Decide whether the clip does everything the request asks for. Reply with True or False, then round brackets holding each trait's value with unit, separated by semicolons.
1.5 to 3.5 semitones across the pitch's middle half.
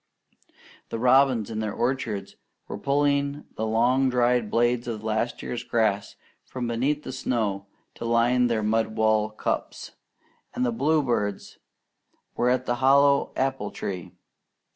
True (3.1 semitones)